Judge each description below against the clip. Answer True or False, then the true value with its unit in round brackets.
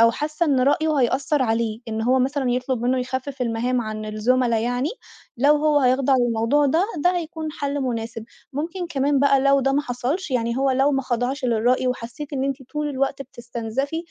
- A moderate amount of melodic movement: True (3.0 semitones)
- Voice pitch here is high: True (260 Hz)